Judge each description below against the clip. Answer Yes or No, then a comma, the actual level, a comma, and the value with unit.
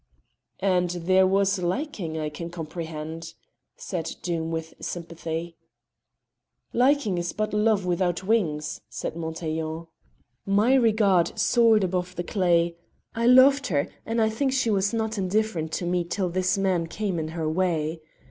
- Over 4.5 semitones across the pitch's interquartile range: No, average, 4.2 semitones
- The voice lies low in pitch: No, medium, 180 Hz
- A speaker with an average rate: Yes, average, 145 wpm